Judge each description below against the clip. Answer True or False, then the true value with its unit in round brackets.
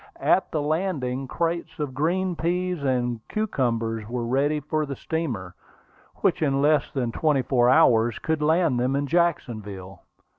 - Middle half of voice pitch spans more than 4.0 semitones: True (5.1 semitones)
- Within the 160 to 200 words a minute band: False (150 wpm)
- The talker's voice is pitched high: False (140 Hz)